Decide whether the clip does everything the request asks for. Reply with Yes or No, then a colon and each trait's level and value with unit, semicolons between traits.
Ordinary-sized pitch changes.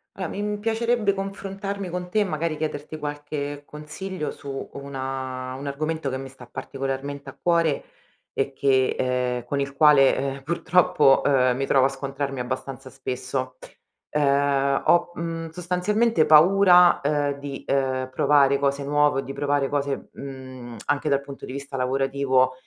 Yes: average, 3.1 semitones